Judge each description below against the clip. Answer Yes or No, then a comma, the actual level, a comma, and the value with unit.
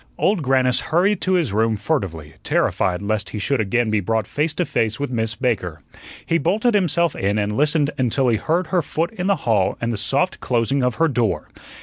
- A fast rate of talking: Yes, fast, 210 wpm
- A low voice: Yes, low, 125 Hz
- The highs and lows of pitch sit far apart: Yes, wide, 7.1 semitones